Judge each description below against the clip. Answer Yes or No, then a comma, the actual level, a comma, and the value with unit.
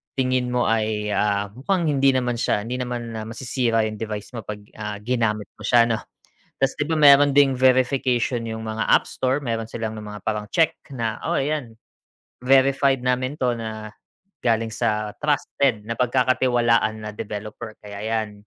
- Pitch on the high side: No, low, 115 Hz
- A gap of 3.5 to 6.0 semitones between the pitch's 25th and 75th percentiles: No, average, 3.1 semitones